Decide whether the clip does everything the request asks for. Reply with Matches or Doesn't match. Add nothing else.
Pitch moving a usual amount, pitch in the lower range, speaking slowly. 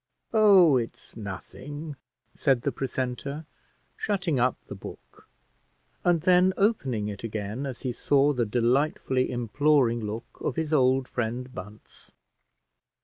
Matches